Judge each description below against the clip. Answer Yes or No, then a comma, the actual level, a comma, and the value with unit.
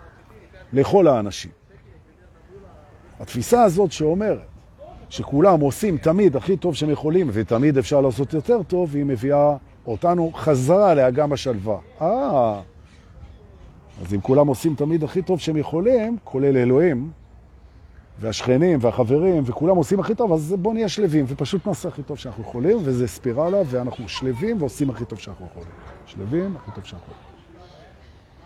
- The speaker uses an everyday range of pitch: No, wide, 7.6 semitones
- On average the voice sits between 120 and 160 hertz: Yes, medium, 140 Hz